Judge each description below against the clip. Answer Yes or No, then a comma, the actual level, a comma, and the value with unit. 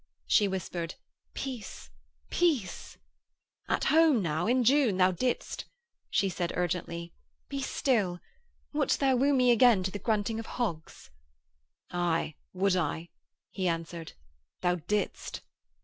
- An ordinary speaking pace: No, slow, 125 wpm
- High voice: Yes, high, 195 Hz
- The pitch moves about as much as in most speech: No, wide, 6.0 semitones